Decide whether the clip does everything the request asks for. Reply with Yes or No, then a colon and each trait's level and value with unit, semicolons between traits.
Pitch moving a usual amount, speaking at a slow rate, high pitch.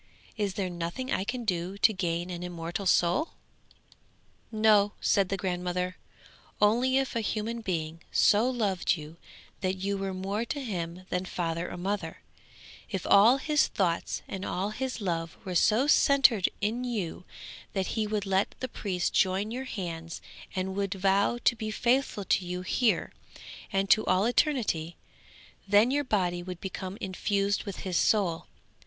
No: average, 3.3 semitones; average, 160 wpm; high, 195 Hz